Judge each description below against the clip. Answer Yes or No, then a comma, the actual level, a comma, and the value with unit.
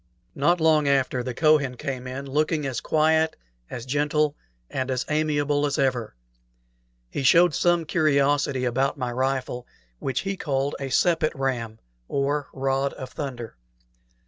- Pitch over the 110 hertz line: Yes, medium, 140 Hz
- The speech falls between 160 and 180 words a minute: No, average, 145 wpm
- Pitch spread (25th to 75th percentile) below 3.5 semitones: Yes, average, 2.7 semitones